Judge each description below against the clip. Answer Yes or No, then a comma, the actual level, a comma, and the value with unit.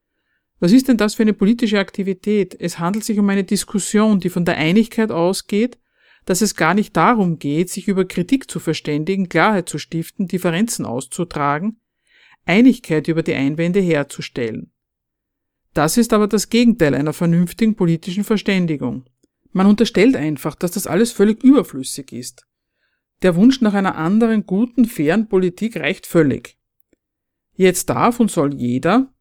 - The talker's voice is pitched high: Yes, high, 195 Hz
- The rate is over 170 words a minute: No, average, 150 wpm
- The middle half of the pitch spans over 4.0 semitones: Yes, average, 4.7 semitones